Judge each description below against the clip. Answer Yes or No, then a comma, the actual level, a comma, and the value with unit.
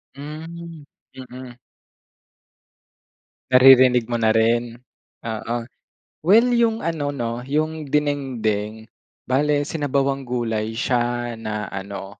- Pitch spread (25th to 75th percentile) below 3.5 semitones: No, average, 4.2 semitones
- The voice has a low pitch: Yes, low, 130 Hz